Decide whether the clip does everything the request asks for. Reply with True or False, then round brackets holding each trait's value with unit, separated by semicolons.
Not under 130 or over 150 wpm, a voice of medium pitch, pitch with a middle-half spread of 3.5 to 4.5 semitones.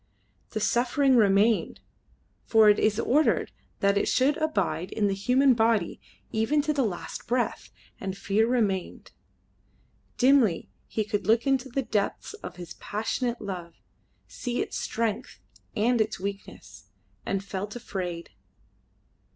False (135 wpm; 220 Hz; 3.9 semitones)